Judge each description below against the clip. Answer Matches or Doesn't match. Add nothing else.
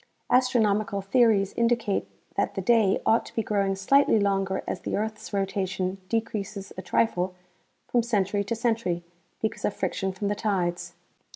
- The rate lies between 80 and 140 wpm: Doesn't match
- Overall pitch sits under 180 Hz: Doesn't match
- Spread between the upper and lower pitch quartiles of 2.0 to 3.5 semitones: Matches